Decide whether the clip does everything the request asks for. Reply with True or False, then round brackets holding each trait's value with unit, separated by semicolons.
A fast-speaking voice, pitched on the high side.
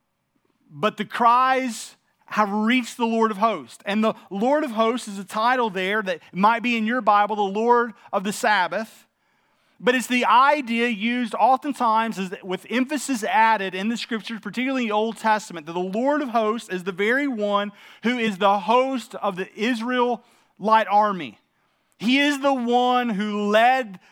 False (170 wpm; 225 Hz)